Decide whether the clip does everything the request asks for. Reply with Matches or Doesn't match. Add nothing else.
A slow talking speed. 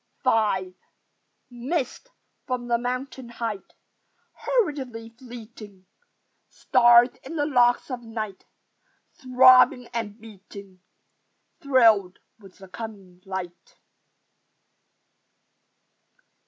Matches